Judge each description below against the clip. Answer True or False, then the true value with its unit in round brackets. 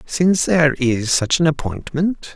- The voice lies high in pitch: False (150 Hz)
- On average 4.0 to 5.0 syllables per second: True (4.5 syllables/s)